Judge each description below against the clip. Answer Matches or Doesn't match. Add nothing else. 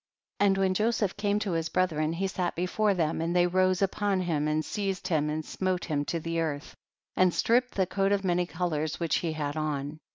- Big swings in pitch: Doesn't match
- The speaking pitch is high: Doesn't match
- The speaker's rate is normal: Doesn't match